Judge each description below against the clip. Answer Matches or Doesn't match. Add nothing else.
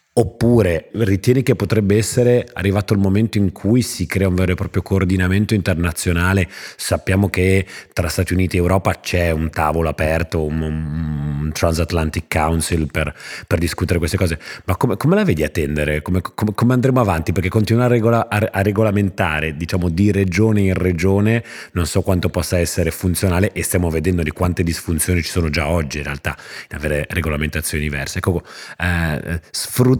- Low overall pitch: Matches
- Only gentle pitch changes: Doesn't match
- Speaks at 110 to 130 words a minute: Doesn't match